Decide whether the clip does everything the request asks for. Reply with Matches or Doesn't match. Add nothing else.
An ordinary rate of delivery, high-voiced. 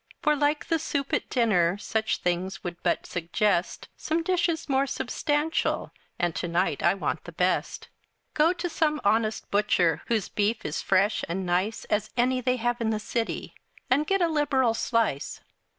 Matches